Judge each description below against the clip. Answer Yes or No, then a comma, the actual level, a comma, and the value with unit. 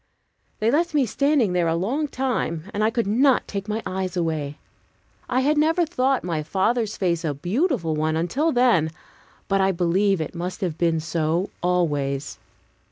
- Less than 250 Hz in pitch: Yes, high, 190 Hz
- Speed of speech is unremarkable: Yes, average, 170 wpm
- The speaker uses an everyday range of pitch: No, wide, 7.1 semitones